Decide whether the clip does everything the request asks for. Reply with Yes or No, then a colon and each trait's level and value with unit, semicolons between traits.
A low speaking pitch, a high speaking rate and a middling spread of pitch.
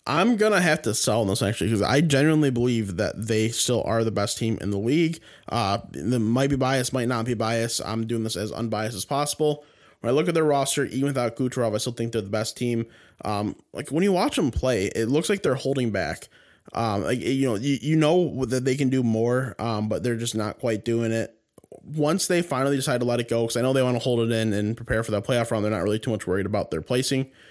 Yes: low, 120 Hz; fast, 255 wpm; average, 3.4 semitones